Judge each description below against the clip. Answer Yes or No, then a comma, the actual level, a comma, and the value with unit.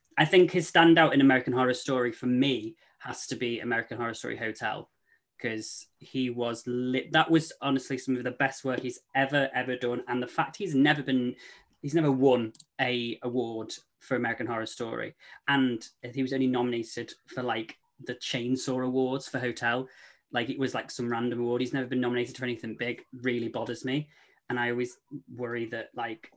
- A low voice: Yes, low, 125 Hz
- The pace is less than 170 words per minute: No, average, 190 wpm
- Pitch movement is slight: Yes, narrow, 1.9 semitones